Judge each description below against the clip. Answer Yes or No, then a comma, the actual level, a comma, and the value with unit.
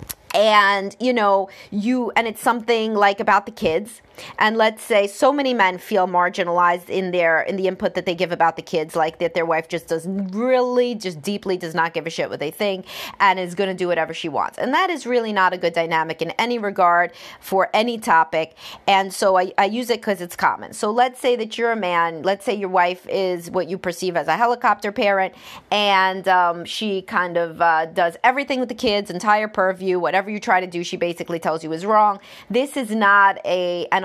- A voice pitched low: No, high, 190 Hz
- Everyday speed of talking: No, fast, 220 wpm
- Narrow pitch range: No, average, 3.7 semitones